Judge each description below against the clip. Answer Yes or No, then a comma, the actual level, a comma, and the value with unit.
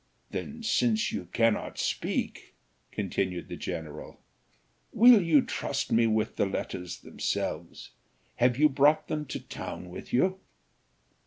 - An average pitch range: No, wide, 7.9 semitones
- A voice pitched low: Yes, low, 120 Hz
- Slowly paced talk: Yes, slow, 130 wpm